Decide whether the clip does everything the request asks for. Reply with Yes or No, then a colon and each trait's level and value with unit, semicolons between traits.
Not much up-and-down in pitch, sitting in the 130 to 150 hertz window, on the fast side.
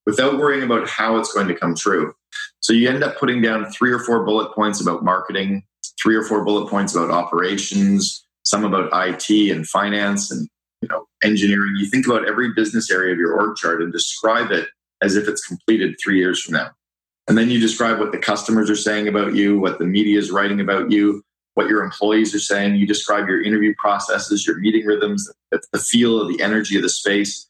No: narrow, 1.9 semitones; low, 105 Hz; fast, 215 wpm